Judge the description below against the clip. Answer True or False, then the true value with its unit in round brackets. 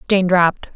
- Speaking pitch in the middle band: True (180 Hz)